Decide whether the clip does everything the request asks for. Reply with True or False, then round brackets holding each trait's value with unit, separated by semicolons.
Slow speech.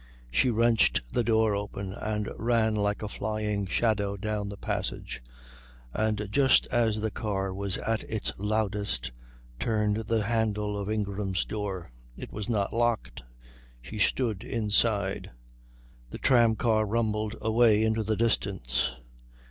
True (130 wpm)